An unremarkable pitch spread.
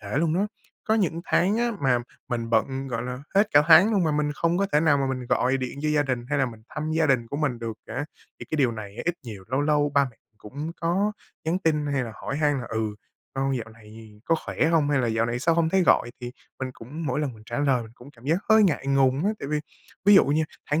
Yes: average, 4.7 semitones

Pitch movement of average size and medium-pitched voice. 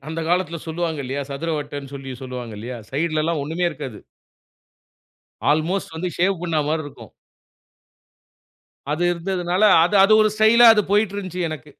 Yes: average, 4.2 semitones; medium, 165 Hz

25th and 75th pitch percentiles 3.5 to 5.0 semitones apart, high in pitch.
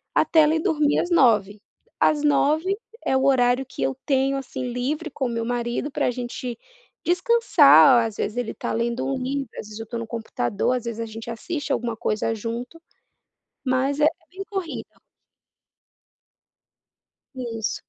Yes: average, 4.0 semitones; very high, 255 Hz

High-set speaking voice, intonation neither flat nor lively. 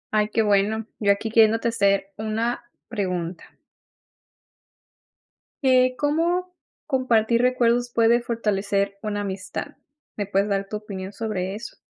Yes: high, 215 Hz; average, 3.0 semitones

